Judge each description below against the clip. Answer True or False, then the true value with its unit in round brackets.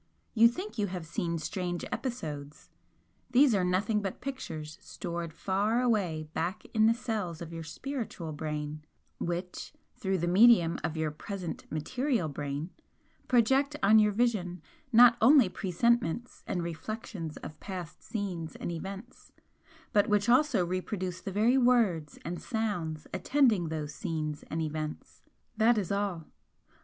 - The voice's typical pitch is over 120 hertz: True (185 Hz)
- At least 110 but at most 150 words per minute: True (140 wpm)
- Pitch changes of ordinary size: False (5.7 semitones)